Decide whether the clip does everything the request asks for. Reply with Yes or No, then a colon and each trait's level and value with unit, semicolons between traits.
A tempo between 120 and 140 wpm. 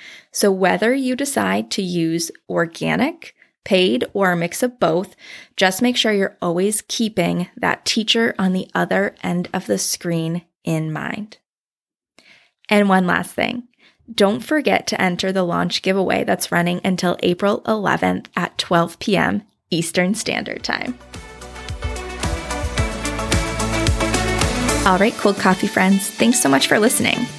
Yes: slow, 135 wpm